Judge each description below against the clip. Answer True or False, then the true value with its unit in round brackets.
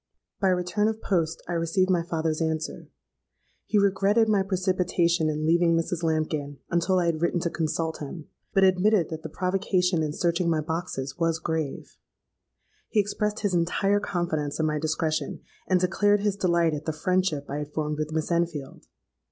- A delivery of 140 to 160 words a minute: False (175 wpm)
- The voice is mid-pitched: True (170 Hz)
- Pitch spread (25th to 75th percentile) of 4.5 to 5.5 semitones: False (2.9 semitones)